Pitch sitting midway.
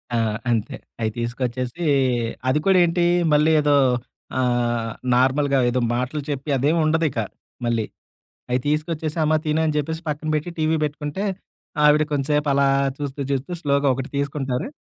Yes: medium, 145 Hz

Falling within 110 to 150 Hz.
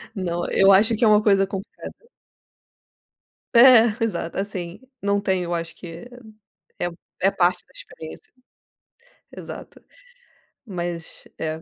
No: high, 190 Hz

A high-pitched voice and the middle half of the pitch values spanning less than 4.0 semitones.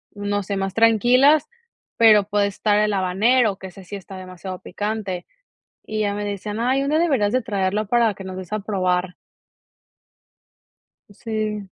Yes: high, 205 Hz; narrow, 2.4 semitones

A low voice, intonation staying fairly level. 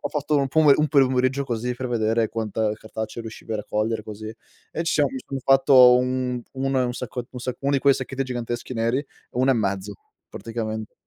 No: low, 125 Hz; average, 3.0 semitones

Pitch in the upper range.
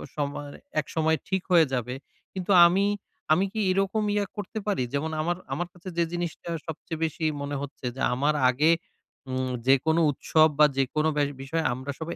No: medium, 160 Hz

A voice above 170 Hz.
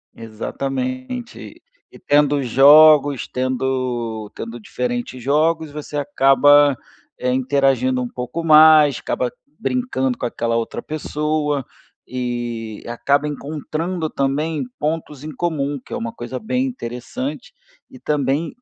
No: medium, 140 Hz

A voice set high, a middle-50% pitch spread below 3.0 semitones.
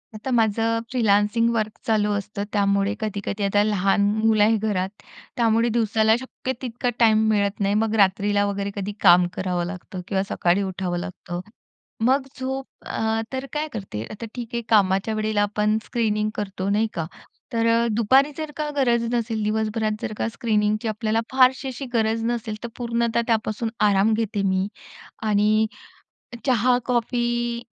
Yes: high, 215 Hz; narrow, 2.4 semitones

